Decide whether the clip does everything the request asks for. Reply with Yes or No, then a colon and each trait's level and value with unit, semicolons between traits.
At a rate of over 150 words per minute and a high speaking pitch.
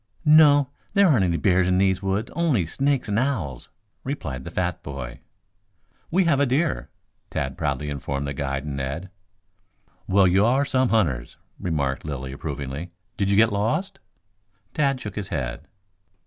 No: average, 160 wpm; very low, 95 Hz